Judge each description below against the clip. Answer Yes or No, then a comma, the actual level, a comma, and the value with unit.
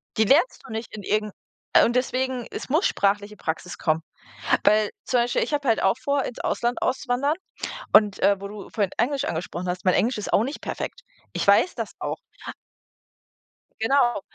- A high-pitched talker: Yes, high, 220 Hz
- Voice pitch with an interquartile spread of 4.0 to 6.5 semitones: Yes, average, 4.3 semitones